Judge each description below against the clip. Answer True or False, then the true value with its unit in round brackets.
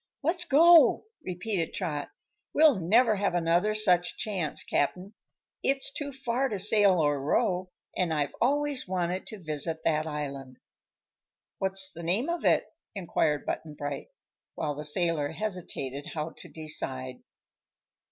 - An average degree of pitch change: False (6.0 semitones)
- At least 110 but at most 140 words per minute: True (135 wpm)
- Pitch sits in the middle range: True (180 Hz)